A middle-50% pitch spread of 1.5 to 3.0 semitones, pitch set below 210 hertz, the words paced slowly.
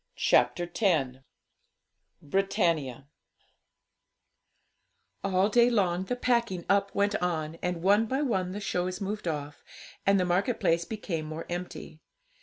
No: average, 3.6 semitones; medium, 185 Hz; slow, 125 wpm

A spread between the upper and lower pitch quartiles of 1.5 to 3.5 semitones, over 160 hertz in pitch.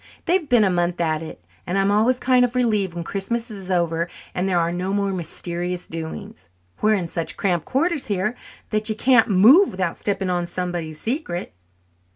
No: average, 4.3 semitones; high, 190 Hz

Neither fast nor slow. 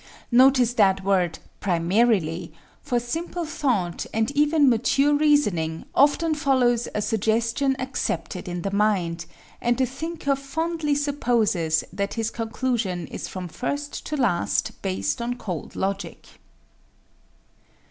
No: slow, 120 wpm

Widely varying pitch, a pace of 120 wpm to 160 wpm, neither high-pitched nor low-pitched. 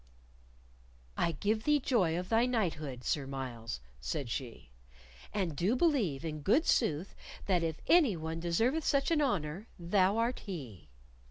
Yes: wide, 7.5 semitones; average, 150 wpm; medium, 175 Hz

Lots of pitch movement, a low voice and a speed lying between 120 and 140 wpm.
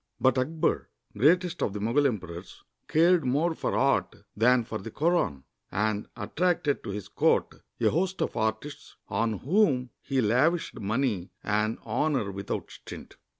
No: wide, 6.5 semitones; low, 125 Hz; average, 150 wpm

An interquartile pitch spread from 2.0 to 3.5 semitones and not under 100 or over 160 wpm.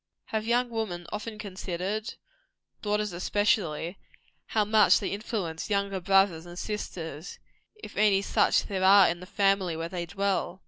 Yes: average, 3.1 semitones; average, 145 wpm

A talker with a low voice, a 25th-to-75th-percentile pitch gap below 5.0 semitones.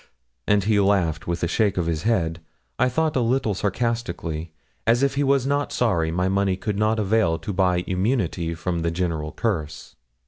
No: very low, 95 Hz; average, 5.3 semitones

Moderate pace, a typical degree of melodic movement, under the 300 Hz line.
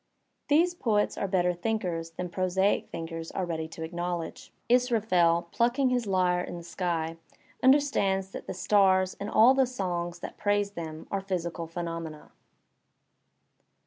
Yes: average, 150 wpm; average, 3.6 semitones; medium, 185 Hz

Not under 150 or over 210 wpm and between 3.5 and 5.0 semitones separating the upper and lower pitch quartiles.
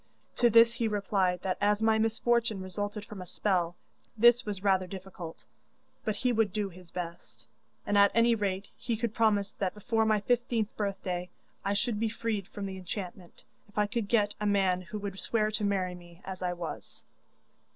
No: average, 190 wpm; average, 2.9 semitones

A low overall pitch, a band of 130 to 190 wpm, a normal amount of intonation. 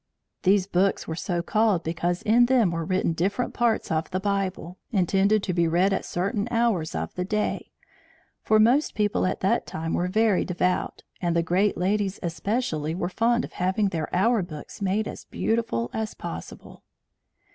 No: high, 190 Hz; average, 180 wpm; average, 3.7 semitones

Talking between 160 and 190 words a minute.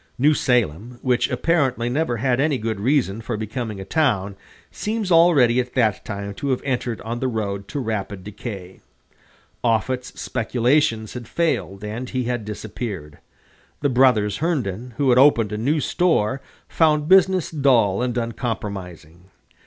No: average, 150 wpm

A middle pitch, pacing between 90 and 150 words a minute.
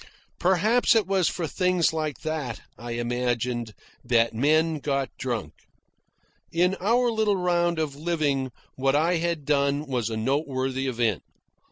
Yes: medium, 145 Hz; average, 140 wpm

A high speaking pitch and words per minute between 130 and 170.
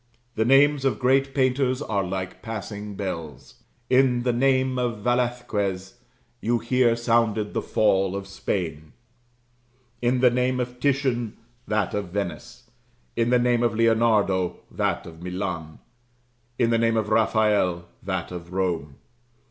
No: low, 115 Hz; average, 140 wpm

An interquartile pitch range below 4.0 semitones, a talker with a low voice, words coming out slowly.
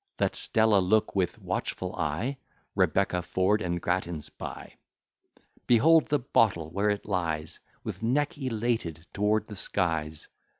No: average, 4.5 semitones; low, 100 Hz; slow, 130 wpm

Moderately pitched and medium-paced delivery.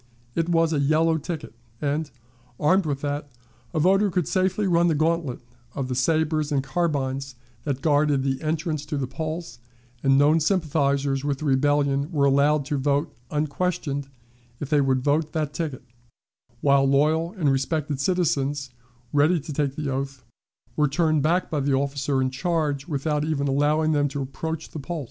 Yes: medium, 145 Hz; average, 170 wpm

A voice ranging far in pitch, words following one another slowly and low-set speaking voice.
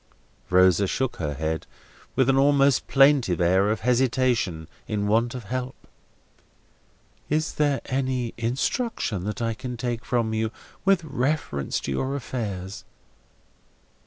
No: average, 4.9 semitones; slow, 130 wpm; low, 120 Hz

